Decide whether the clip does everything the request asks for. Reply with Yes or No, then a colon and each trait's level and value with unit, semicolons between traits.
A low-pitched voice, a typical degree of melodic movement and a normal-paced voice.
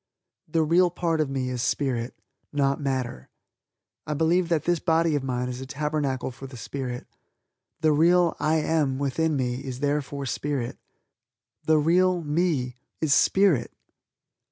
No: medium, 145 Hz; average, 3.6 semitones; average, 150 wpm